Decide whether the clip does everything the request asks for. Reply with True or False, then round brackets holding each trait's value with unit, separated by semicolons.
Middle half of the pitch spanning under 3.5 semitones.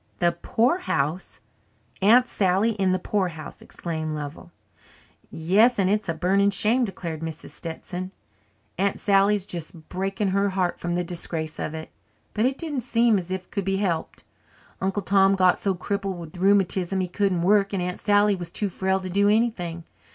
True (2.7 semitones)